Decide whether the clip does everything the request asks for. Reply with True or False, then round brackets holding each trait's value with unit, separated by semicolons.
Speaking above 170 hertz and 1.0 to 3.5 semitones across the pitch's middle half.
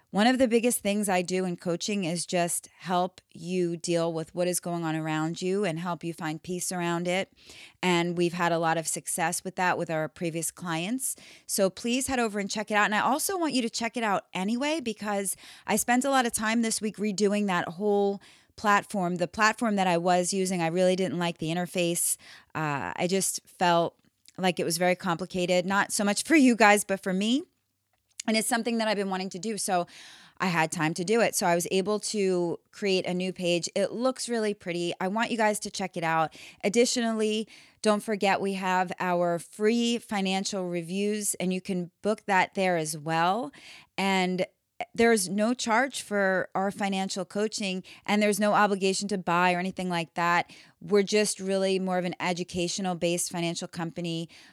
True (190 Hz; 3.2 semitones)